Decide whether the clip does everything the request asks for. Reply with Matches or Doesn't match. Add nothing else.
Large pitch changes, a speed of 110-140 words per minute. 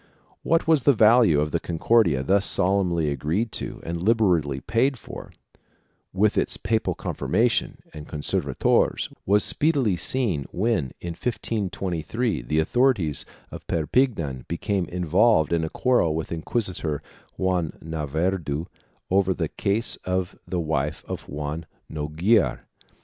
Matches